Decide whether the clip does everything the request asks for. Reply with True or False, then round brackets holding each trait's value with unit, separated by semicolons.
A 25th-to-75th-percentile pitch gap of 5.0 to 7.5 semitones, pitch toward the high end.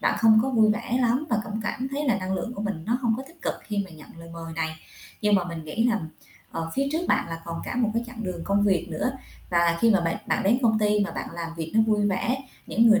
True (5.4 semitones; 210 Hz)